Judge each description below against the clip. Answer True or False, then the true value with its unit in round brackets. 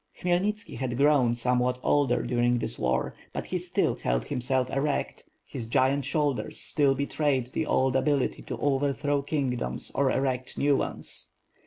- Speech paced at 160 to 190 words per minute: False (150 wpm)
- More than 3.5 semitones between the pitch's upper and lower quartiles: False (2.5 semitones)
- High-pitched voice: False (135 Hz)